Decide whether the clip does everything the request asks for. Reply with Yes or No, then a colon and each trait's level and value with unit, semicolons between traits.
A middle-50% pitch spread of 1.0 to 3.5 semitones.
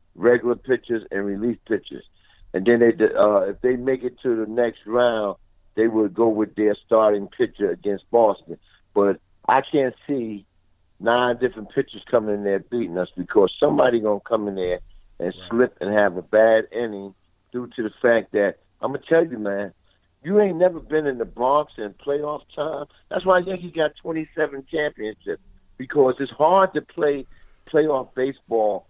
No: average, 5.3 semitones